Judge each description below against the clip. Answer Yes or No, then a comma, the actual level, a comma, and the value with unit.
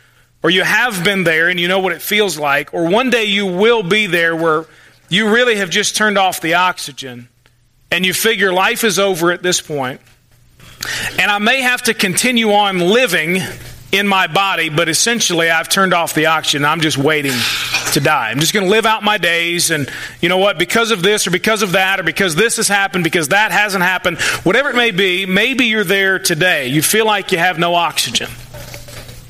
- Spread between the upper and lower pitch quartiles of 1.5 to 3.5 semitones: No, average, 4.7 semitones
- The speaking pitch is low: No, medium, 185 Hz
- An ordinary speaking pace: No, fast, 210 wpm